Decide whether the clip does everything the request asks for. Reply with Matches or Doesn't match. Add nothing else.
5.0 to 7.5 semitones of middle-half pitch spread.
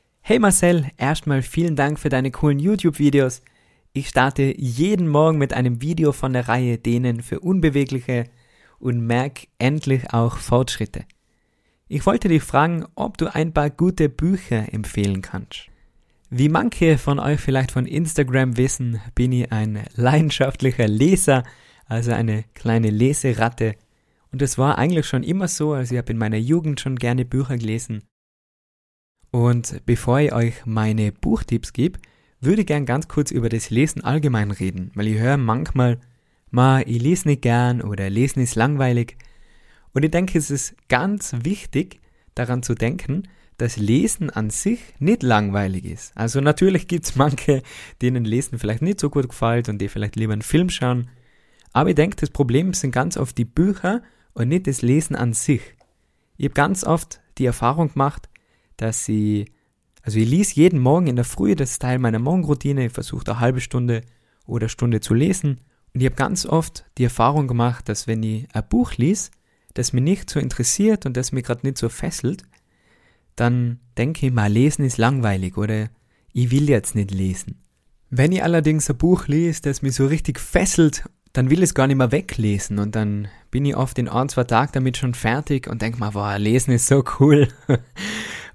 Doesn't match